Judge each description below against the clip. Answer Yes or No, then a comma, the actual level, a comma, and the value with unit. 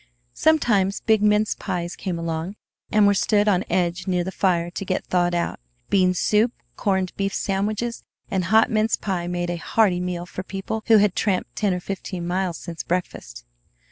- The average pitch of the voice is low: No, high, 190 Hz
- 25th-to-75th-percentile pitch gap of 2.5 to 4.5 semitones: Yes, average, 2.9 semitones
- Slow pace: No, average, 180 wpm